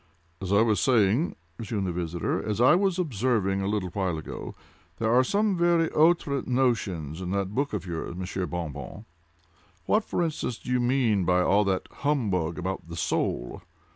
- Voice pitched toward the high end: No, low, 105 Hz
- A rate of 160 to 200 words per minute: Yes, average, 175 wpm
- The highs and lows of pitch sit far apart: Yes, wide, 6.3 semitones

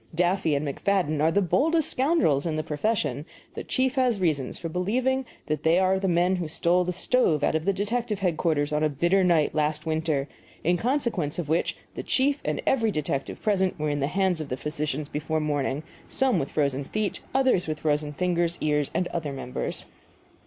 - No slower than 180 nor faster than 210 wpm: Yes, average, 195 wpm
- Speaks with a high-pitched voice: No, medium, 170 Hz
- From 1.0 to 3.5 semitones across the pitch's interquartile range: No, average, 4.7 semitones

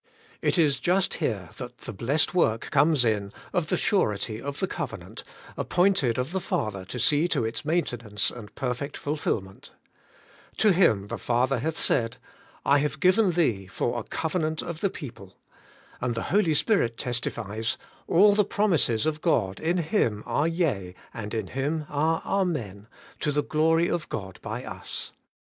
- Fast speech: No, average, 165 wpm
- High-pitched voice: No, medium, 145 Hz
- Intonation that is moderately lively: No, wide, 7.0 semitones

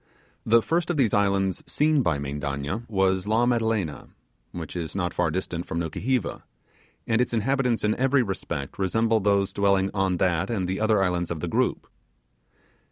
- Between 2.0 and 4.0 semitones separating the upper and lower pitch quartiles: No, average, 4.6 semitones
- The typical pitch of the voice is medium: No, low, 100 Hz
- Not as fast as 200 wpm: Yes, average, 165 wpm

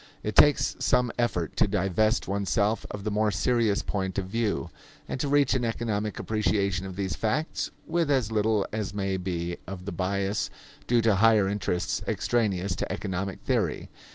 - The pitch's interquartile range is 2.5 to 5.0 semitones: Yes, average, 2.8 semitones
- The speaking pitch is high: No, low, 105 Hz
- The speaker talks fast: No, average, 170 wpm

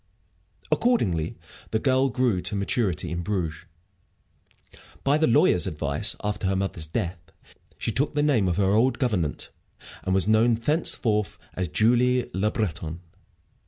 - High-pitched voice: No, low, 105 Hz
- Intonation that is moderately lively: No, wide, 5.7 semitones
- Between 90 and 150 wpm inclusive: Yes, average, 140 wpm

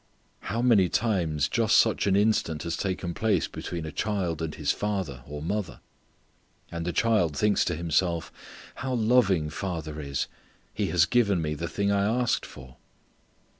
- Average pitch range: Yes, average, 4.9 semitones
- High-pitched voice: No, very low, 90 Hz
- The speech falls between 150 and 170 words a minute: Yes, average, 165 wpm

